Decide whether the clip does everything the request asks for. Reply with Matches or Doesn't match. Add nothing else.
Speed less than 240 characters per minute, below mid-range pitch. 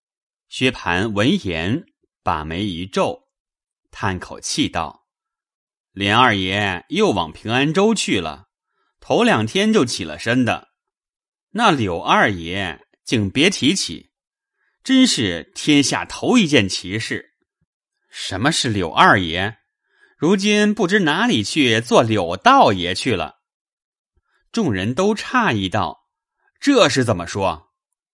Doesn't match